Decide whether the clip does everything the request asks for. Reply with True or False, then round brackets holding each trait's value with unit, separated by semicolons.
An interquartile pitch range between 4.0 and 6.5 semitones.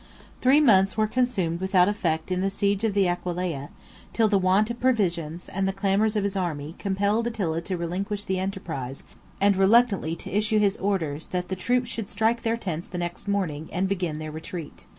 False (3.3 semitones)